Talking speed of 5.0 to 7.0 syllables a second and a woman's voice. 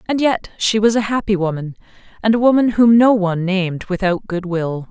Yes: 5.4 syllables/s; female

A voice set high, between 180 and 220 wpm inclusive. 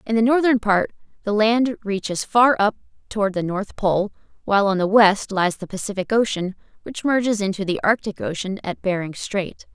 Yes: high, 205 Hz; average, 185 wpm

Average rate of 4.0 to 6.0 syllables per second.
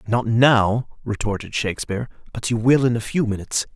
Yes: 5.7 syllables/s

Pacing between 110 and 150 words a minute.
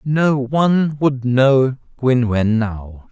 Yes: slow, 135 wpm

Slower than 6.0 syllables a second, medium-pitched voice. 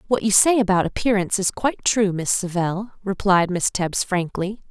No: 5.1 syllables/s; high, 195 Hz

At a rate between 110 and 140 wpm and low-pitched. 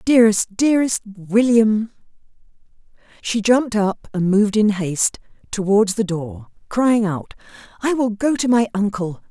No: slow, 135 wpm; high, 210 Hz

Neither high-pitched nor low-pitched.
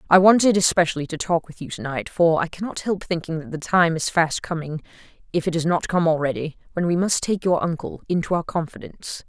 Yes: medium, 170 Hz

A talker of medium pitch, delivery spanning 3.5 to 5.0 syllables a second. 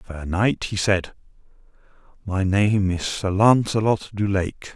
No: low, 100 Hz; 3.6 syllables/s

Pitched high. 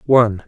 No: low, 115 Hz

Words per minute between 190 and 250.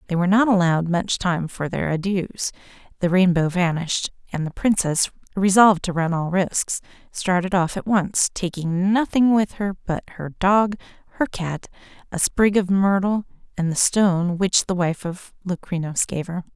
No: average, 170 wpm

